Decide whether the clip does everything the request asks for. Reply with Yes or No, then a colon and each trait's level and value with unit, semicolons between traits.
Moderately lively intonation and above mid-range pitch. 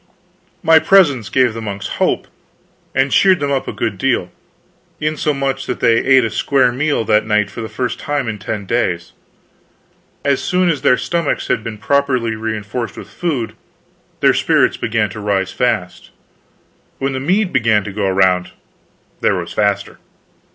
No: average, 4.9 semitones; low, 120 Hz